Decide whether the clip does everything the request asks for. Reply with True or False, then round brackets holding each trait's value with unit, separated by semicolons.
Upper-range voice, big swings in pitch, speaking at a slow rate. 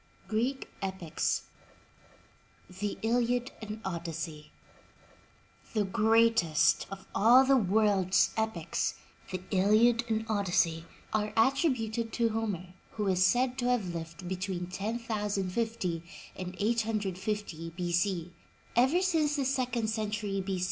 False (210 Hz; 4.0 semitones; 120 wpm)